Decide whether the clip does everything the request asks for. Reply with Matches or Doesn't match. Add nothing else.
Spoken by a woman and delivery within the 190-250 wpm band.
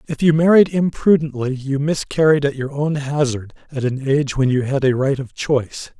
Doesn't match